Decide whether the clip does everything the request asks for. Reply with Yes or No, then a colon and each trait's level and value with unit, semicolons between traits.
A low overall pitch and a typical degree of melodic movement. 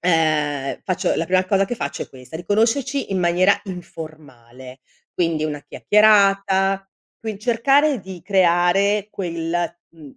No: medium, 180 Hz; average, 3.9 semitones